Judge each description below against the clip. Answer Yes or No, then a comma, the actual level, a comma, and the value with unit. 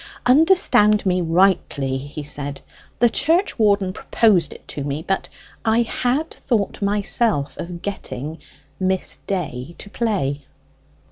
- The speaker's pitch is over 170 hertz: Yes, high, 190 Hz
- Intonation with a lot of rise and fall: Yes, wide, 7.0 semitones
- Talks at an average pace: No, slow, 125 wpm